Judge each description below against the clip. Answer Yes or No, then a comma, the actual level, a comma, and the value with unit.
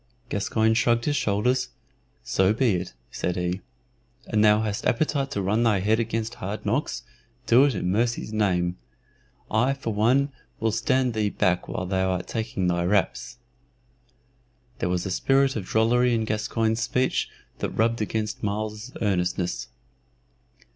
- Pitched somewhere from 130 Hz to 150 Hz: No, low, 110 Hz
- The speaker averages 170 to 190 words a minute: No, average, 150 wpm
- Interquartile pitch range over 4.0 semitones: No, average, 3.5 semitones